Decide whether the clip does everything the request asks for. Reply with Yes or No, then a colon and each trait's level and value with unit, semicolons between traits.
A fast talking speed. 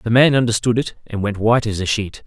Yes: fast, 265 wpm